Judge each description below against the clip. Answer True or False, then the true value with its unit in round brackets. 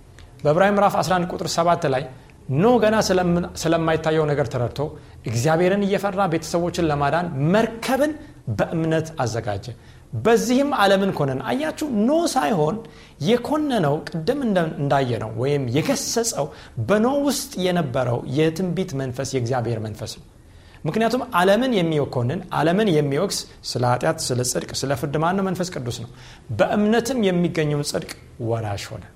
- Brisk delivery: True (115 wpm)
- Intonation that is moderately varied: False (7.3 semitones)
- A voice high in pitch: False (160 Hz)